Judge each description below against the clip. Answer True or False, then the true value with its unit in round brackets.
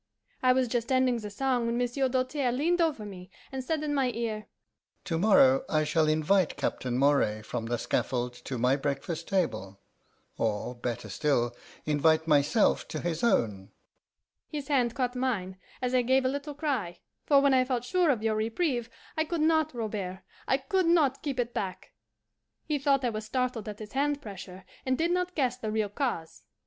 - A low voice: False (235 Hz)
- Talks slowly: False (185 wpm)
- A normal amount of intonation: False (7.8 semitones)